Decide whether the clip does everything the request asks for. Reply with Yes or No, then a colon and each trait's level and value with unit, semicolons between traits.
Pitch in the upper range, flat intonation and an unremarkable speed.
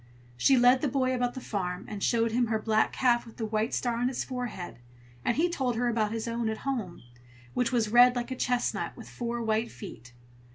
No: high, 235 Hz; narrow, 2.2 semitones; fast, 220 wpm